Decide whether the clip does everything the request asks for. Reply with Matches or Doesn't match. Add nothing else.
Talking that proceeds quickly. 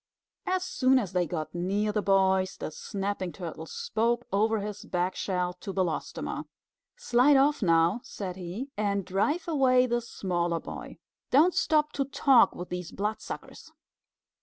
Doesn't match